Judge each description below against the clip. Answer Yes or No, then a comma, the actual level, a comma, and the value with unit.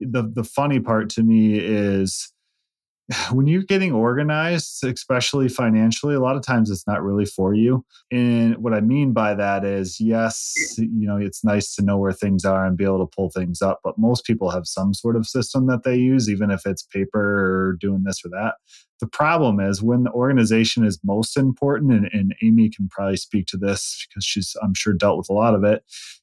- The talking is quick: Yes, fast, 215 wpm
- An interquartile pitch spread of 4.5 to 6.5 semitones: No, average, 3.7 semitones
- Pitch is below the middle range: Yes, low, 110 Hz